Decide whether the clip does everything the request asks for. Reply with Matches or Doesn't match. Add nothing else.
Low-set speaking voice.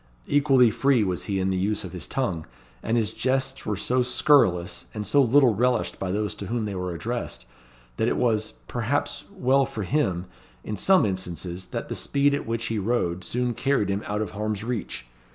Matches